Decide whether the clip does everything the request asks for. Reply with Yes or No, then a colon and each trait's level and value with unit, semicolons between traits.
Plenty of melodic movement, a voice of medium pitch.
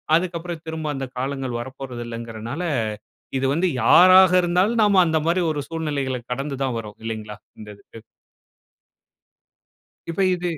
Yes: wide, 6.2 semitones; medium, 145 Hz